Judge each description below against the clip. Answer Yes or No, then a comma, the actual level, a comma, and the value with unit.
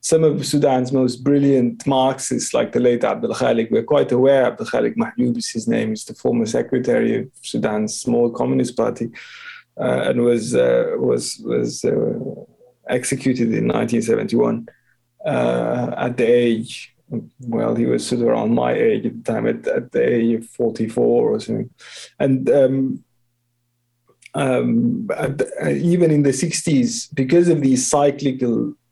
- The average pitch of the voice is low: Yes, low, 130 Hz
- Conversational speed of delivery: Yes, average, 155 wpm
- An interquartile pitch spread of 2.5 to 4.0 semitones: No, wide, 5.6 semitones